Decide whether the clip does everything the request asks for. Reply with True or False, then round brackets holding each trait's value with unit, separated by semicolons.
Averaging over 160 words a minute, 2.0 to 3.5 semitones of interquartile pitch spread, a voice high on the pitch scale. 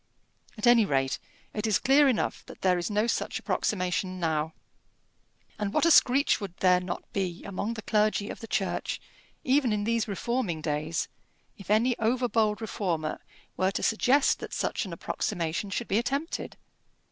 False (170 wpm; 4.4 semitones; 210 Hz)